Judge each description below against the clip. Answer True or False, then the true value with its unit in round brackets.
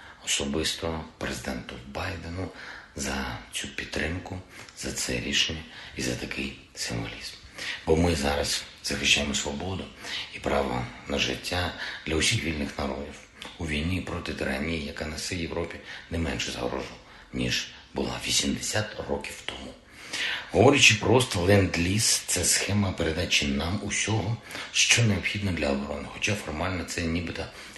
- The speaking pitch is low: True (80 Hz)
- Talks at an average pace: True (120 wpm)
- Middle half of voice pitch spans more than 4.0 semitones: True (4.9 semitones)